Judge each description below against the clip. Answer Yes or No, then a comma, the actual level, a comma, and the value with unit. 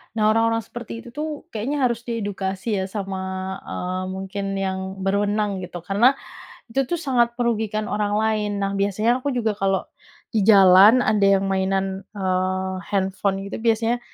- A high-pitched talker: Yes, high, 205 Hz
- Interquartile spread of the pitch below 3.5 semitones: Yes, average, 2.8 semitones